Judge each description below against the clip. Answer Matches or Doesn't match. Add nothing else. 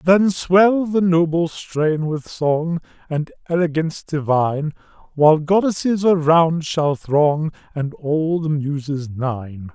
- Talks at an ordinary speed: Doesn't match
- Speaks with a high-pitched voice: Doesn't match